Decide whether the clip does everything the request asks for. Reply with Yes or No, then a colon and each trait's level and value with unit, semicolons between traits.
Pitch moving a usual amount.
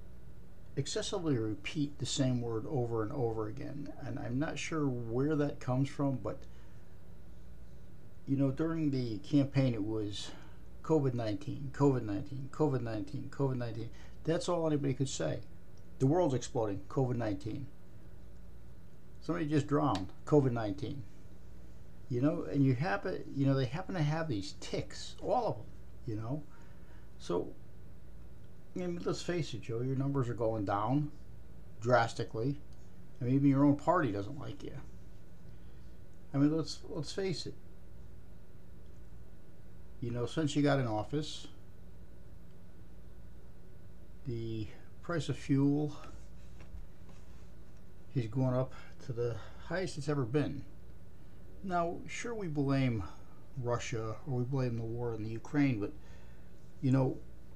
No: wide, 5.7 semitones